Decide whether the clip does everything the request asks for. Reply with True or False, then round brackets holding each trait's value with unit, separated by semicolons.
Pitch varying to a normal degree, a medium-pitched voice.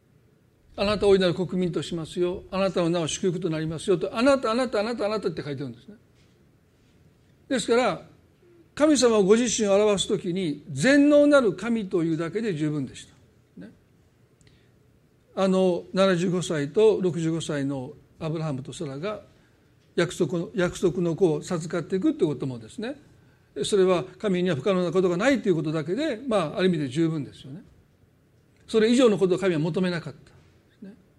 True (4.8 semitones; 180 Hz)